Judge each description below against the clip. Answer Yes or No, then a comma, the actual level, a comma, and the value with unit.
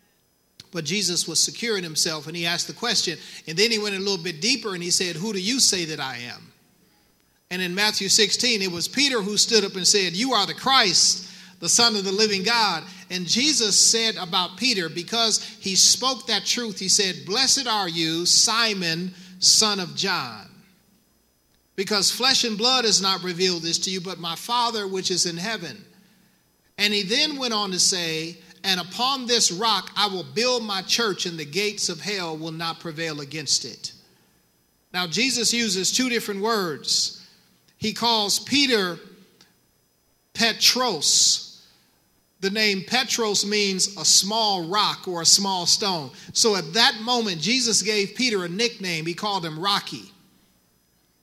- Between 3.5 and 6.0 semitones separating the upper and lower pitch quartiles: Yes, average, 4.0 semitones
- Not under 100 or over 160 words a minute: No, average, 170 wpm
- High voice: Yes, high, 195 Hz